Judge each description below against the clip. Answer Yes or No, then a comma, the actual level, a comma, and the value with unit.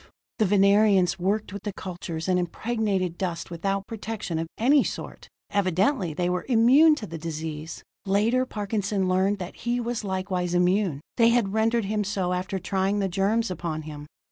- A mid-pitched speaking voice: No, high, 195 Hz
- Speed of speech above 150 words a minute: Yes, average, 170 wpm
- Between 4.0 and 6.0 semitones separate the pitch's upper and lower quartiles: No, average, 3.4 semitones